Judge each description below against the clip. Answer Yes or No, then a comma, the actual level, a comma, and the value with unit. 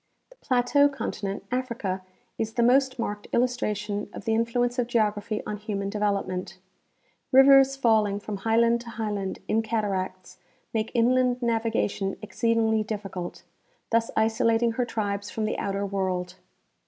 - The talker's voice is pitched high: Yes, high, 220 Hz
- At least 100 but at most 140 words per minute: Yes, slow, 135 wpm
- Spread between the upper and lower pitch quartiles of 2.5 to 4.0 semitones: Yes, average, 2.8 semitones